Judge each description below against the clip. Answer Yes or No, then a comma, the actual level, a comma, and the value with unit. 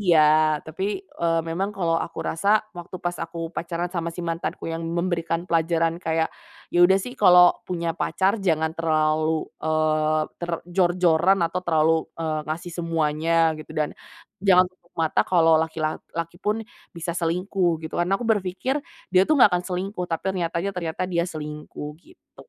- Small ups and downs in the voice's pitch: Yes, narrow, 2.1 semitones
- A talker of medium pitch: Yes, medium, 170 Hz